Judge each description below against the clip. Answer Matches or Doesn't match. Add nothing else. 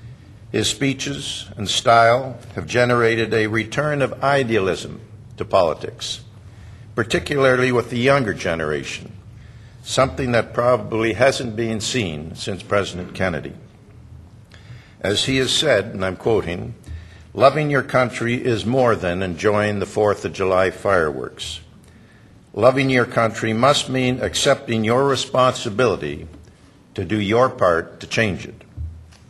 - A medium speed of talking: Doesn't match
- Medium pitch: Doesn't match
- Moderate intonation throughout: Matches